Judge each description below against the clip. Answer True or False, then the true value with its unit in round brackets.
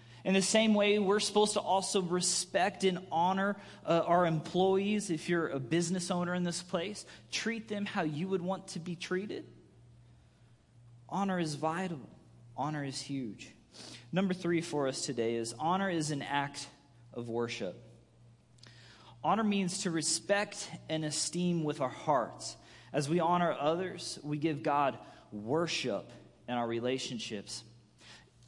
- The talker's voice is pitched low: False (160 Hz)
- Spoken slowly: False (145 wpm)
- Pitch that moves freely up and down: True (7.1 semitones)